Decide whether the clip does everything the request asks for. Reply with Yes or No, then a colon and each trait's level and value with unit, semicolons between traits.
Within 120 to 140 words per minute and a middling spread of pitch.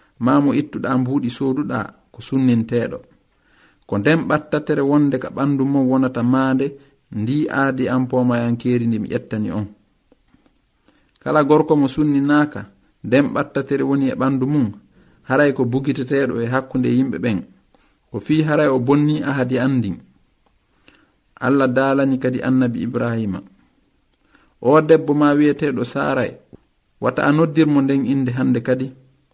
No: slow, 135 wpm; narrow, 2.2 semitones